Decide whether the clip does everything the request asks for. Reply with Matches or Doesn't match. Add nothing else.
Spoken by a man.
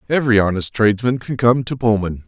Matches